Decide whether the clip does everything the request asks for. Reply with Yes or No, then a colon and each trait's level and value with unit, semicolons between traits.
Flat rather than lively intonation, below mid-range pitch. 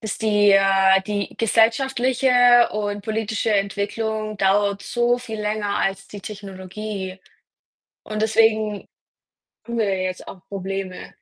No: narrow, 2.1 semitones; high, 210 Hz